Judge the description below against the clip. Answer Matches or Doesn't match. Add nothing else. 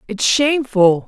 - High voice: Matches